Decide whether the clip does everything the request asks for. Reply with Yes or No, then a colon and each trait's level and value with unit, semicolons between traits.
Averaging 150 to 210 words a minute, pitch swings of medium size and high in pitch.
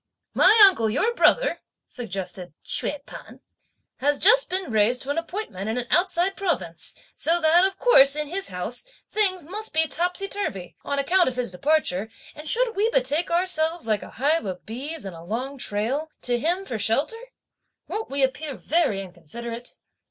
No: average, 175 wpm; wide, 8.0 semitones; very high, 290 Hz